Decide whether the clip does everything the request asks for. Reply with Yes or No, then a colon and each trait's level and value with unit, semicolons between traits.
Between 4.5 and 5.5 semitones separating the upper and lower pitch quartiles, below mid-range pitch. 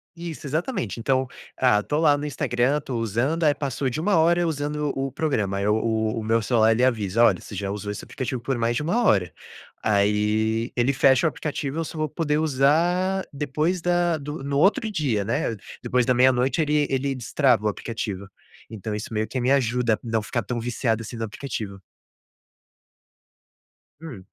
Yes: average, 5.0 semitones; low, 130 Hz